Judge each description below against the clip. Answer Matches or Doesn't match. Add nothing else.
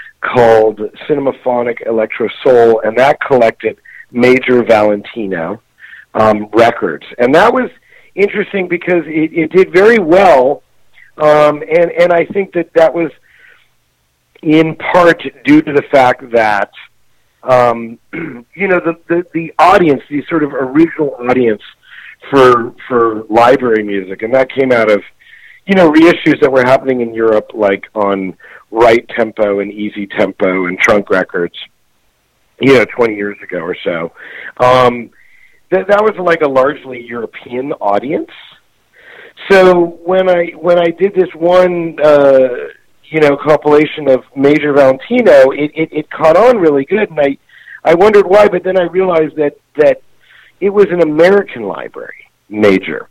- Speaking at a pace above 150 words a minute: Doesn't match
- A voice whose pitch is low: Doesn't match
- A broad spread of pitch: Matches